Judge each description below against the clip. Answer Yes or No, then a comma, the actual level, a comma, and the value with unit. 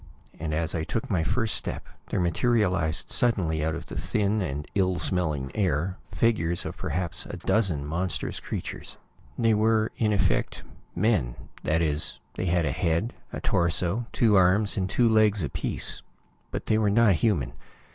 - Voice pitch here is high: No, very low, 90 Hz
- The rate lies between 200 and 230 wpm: No, average, 165 wpm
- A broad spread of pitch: No, average, 4.9 semitones